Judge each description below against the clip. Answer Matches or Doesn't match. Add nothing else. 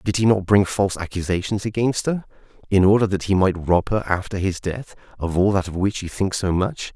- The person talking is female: Doesn't match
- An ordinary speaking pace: Doesn't match